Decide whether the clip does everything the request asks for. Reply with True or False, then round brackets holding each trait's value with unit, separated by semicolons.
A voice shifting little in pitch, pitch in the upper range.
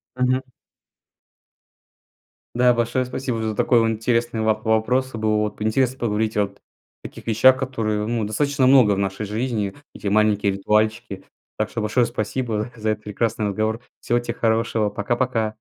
False (2.3 semitones; 110 Hz)